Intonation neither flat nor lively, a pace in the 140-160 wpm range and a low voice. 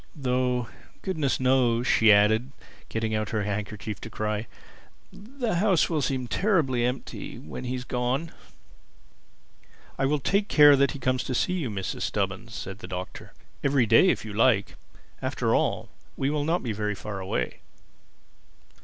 Yes: average, 4.7 semitones; average, 155 wpm; low, 125 Hz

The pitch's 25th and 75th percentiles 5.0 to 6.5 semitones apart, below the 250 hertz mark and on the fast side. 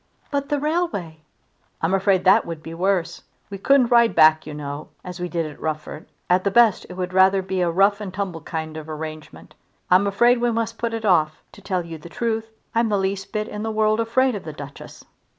Yes: wide, 5.4 semitones; high, 190 Hz; fast, 220 wpm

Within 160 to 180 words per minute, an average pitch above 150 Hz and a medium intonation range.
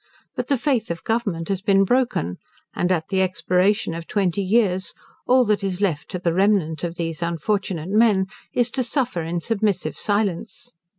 Yes: average, 175 wpm; high, 190 Hz; average, 4.0 semitones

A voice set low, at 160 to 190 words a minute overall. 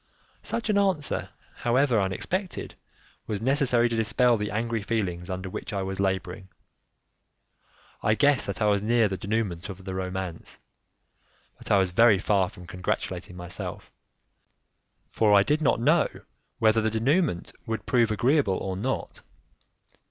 No: low, 105 Hz; average, 145 wpm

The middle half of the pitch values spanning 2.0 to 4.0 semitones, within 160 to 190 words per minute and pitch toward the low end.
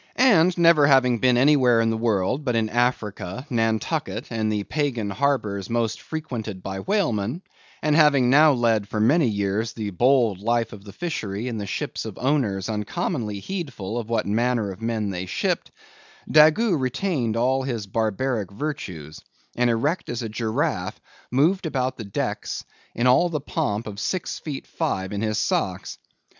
No: average, 5.0 semitones; average, 165 wpm; low, 120 Hz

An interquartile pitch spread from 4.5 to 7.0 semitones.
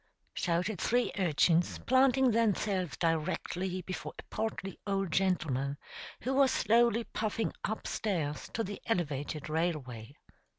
Yes: wide, 5.4 semitones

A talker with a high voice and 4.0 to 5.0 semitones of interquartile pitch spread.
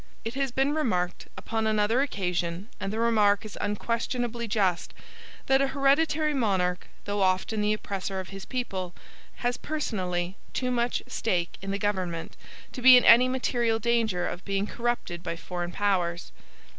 Yes: high, 210 Hz; average, 4.6 semitones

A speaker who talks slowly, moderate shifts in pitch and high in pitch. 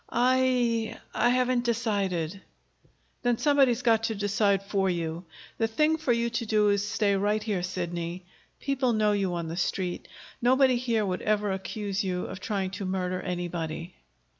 No: average, 165 wpm; average, 4.2 semitones; high, 205 Hz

